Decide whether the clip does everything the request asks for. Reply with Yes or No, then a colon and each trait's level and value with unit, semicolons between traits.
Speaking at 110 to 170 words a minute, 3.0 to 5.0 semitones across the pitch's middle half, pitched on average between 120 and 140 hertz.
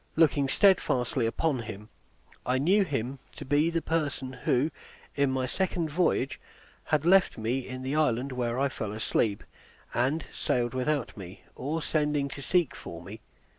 Yes: average, 160 wpm; average, 4.1 semitones; low, 135 Hz